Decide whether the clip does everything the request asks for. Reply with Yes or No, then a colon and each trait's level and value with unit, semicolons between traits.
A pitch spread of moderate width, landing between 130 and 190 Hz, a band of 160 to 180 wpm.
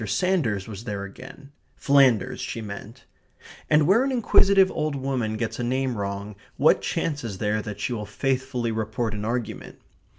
No: average, 4.5 semitones; low, 120 Hz; average, 165 wpm